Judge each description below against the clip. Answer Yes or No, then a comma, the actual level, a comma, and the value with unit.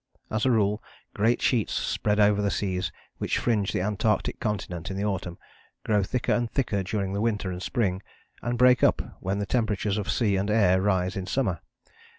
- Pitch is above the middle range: No, low, 105 Hz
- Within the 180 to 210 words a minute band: Yes, average, 190 wpm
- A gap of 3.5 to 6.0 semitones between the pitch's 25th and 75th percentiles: No, narrow, 2.6 semitones